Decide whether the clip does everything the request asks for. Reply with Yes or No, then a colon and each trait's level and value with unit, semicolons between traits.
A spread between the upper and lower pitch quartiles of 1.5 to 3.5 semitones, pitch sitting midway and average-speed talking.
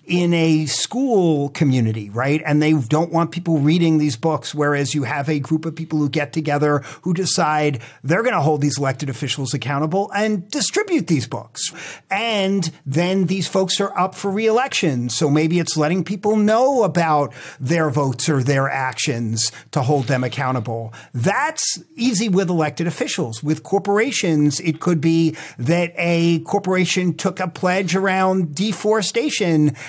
No: average, 4.4 semitones; medium, 160 Hz; average, 160 wpm